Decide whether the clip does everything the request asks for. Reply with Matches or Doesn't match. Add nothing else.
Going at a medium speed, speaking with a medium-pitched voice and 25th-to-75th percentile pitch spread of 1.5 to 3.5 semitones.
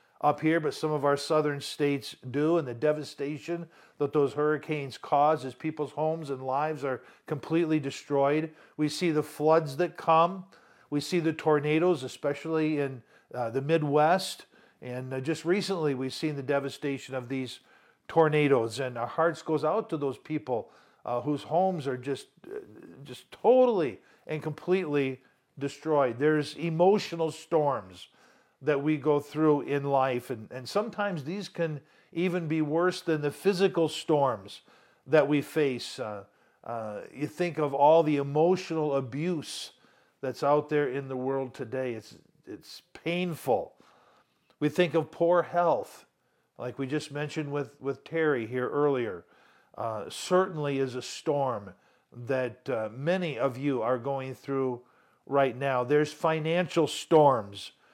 Matches